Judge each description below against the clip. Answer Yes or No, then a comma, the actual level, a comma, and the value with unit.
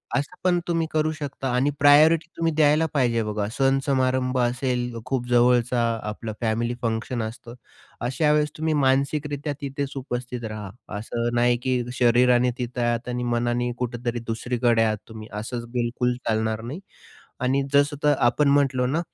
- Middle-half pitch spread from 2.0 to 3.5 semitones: Yes, average, 3.0 semitones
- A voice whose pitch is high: No, low, 125 Hz